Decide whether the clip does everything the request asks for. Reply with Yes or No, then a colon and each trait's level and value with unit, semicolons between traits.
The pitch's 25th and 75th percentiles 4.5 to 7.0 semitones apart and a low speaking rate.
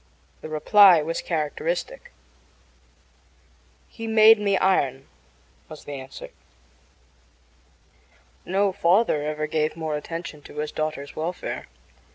Yes: average, 4.8 semitones; slow, 105 wpm